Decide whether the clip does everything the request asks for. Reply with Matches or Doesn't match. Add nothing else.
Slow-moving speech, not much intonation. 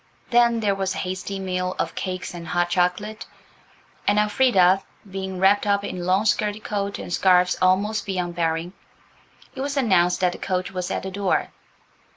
Doesn't match